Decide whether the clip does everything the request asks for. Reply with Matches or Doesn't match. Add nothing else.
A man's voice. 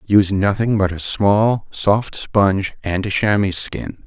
Matches